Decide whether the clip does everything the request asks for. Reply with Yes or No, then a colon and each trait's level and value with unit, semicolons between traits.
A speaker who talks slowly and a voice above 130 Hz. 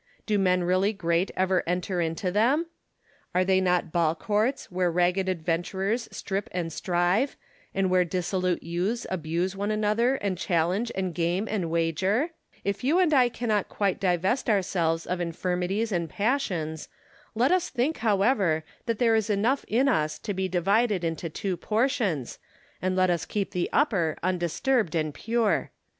No: average, 160 wpm; high, 190 Hz